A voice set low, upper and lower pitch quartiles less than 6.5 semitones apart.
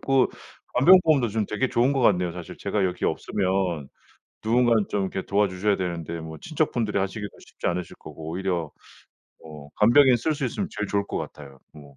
Yes: low, 100 Hz; wide, 5.6 semitones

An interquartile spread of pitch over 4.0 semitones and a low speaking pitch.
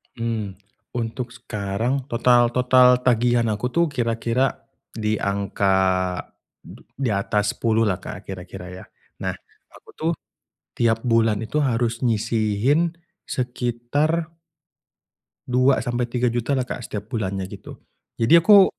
No: average, 2.9 semitones; low, 115 Hz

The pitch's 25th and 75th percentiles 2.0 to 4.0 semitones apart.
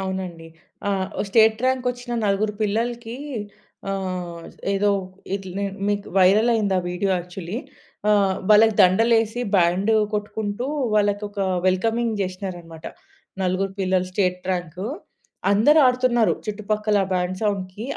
Yes: average, 2.9 semitones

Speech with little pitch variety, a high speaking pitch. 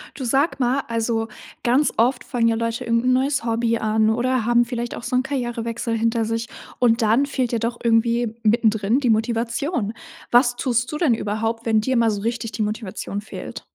Yes: narrow, 1.5 semitones; high, 235 Hz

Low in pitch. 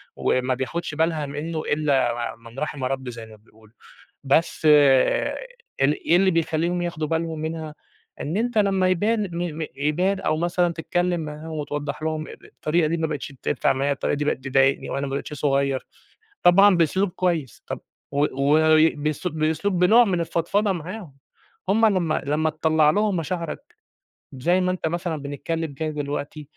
No: medium, 155 Hz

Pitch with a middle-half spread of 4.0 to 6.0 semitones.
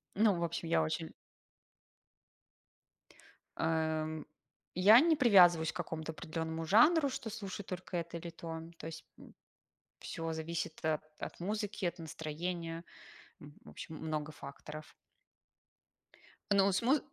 No: average, 3.5 semitones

